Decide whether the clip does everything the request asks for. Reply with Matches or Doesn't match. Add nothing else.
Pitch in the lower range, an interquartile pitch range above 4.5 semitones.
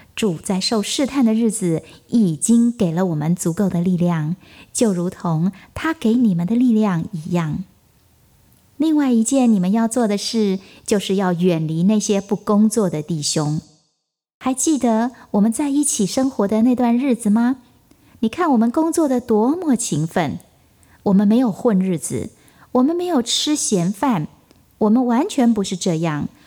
Doesn't match